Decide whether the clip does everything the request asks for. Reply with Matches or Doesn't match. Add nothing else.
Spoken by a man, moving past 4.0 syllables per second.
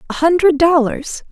Doesn't match